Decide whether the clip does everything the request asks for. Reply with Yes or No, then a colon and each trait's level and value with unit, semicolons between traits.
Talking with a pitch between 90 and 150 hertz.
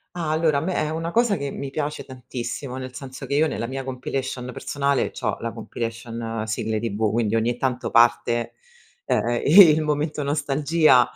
Yes: low, 135 Hz